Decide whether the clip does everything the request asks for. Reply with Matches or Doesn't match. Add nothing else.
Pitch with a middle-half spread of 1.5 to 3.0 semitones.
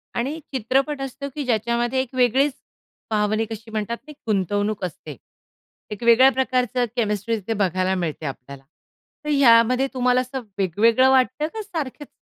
Doesn't match